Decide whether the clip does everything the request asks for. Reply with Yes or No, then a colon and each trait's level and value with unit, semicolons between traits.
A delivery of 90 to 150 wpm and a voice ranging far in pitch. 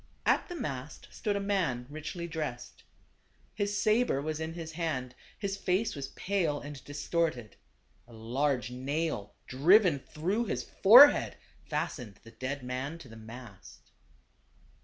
Yes: average, 140 wpm; wide, 6.4 semitones